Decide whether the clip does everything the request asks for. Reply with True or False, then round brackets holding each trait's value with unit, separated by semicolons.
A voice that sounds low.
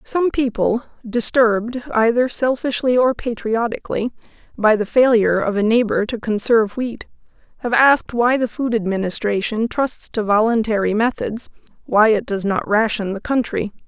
False (230 Hz)